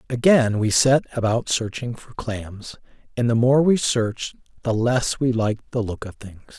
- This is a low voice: Yes, low, 120 Hz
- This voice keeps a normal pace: Yes, average, 180 wpm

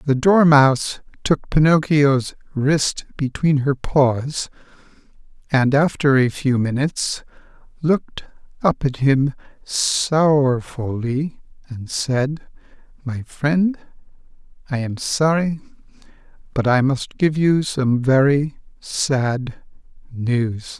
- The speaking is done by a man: Yes, male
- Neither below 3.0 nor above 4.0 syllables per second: Yes, 3.3 syllables/s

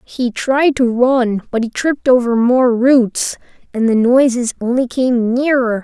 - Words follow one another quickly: No, average, 165 wpm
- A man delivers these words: No, female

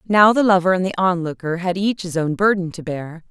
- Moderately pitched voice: Yes, medium, 180 Hz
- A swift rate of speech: Yes, fast, 235 wpm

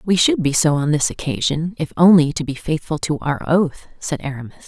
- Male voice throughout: No, female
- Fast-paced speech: Yes, fast, 220 wpm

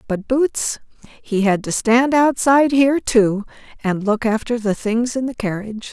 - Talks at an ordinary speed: Yes, average, 170 wpm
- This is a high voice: Yes, high, 235 Hz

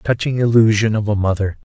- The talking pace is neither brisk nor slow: Yes, average, 170 wpm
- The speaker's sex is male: Yes, male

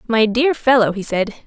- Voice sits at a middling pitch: No, high, 235 Hz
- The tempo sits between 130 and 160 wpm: No, fast, 205 wpm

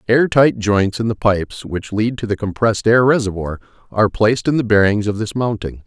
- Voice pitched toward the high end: No, low, 110 Hz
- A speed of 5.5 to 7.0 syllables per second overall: Yes, 5.6 syllables/s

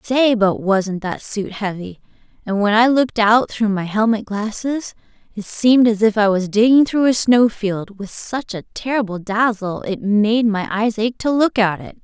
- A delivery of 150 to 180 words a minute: No, average, 200 wpm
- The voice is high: Yes, high, 220 Hz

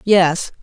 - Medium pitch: Yes, medium, 180 Hz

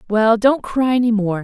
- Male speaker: No, female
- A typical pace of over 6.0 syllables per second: No, 4.9 syllables/s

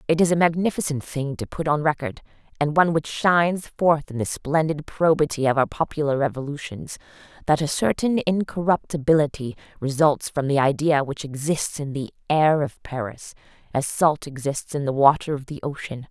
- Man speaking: No, female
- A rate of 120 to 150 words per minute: No, average, 170 wpm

